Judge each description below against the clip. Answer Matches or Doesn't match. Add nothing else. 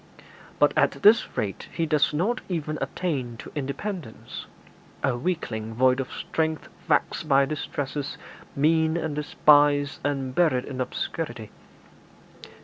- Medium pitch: Matches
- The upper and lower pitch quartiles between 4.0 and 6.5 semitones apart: Doesn't match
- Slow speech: Matches